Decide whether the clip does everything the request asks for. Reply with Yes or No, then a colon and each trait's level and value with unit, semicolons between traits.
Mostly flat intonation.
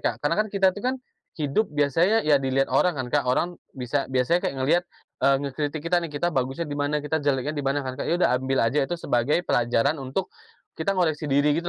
No: average, 4.0 semitones